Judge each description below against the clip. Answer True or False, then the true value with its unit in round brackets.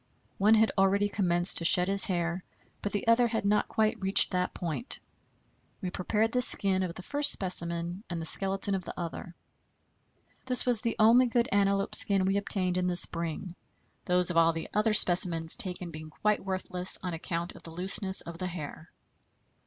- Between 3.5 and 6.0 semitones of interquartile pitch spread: False (2.8 semitones)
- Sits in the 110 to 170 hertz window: False (185 Hz)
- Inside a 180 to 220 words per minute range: True (185 wpm)